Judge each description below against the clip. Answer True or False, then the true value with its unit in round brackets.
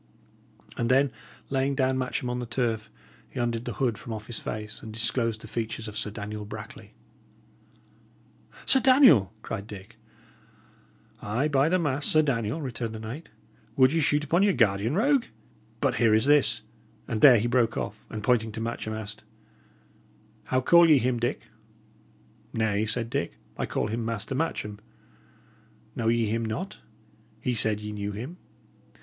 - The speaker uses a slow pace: False (165 wpm)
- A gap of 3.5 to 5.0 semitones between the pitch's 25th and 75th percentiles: True (3.8 semitones)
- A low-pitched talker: True (115 Hz)